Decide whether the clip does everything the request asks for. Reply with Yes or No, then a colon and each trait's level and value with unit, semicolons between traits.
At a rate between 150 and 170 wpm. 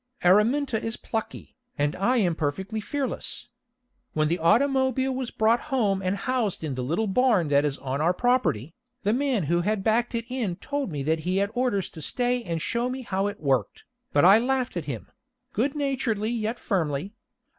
No: average, 190 wpm